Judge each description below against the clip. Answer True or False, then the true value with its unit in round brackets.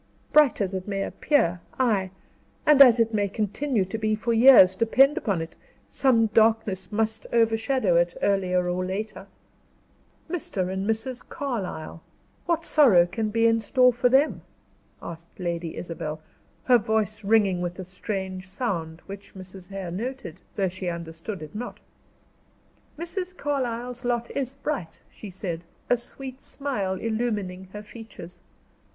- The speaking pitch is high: True (210 Hz)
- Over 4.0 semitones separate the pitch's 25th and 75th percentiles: True (4.7 semitones)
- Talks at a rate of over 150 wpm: False (145 wpm)